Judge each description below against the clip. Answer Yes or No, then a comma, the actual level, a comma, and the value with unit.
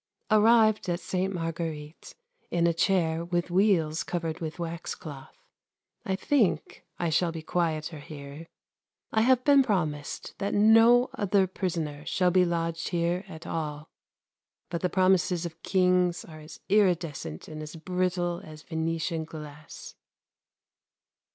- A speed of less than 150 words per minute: Yes, slow, 135 wpm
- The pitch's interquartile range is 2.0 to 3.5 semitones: Yes, average, 2.8 semitones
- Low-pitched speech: No, medium, 170 Hz